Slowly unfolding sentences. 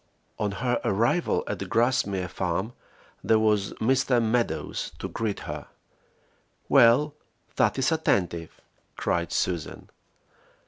Yes: slow, 105 wpm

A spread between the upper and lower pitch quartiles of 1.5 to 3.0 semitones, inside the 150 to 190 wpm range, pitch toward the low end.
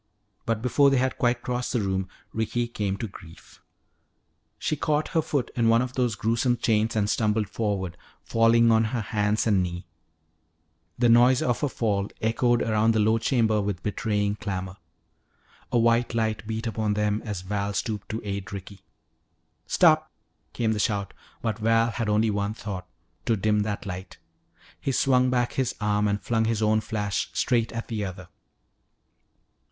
Yes: narrow, 2.4 semitones; average, 170 wpm; low, 110 Hz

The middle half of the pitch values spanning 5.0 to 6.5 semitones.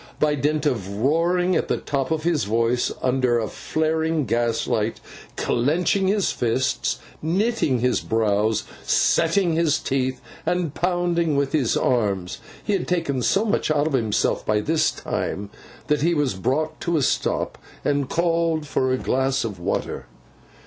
Yes: wide, 5.6 semitones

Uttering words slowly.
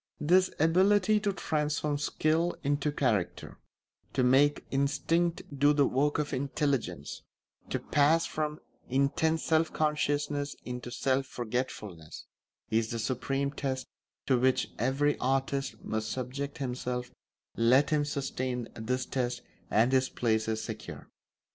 Yes: slow, 125 wpm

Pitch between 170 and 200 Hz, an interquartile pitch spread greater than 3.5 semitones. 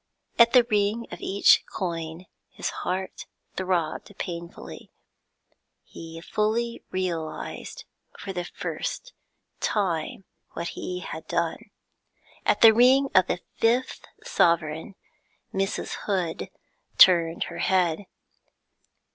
Yes: medium, 185 Hz; average, 4.0 semitones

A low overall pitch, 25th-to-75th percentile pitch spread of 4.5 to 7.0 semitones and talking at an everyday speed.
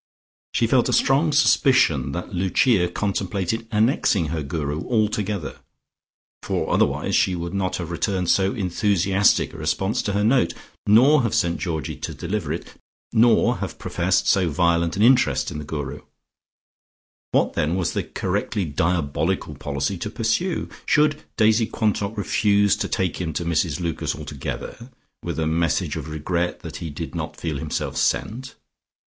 Yes: very low, 90 Hz; average, 4.8 semitones; average, 155 wpm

